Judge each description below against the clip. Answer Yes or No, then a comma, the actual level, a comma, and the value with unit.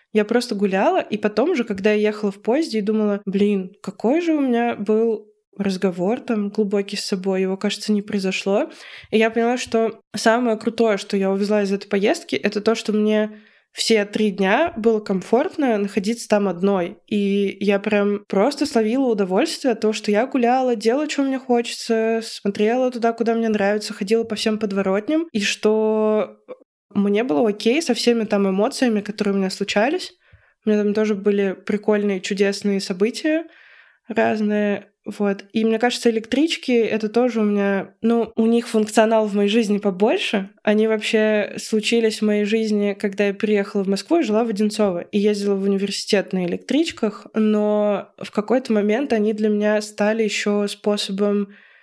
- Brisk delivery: Yes, fast, 170 wpm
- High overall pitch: Yes, high, 215 Hz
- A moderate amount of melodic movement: No, narrow, 1.9 semitones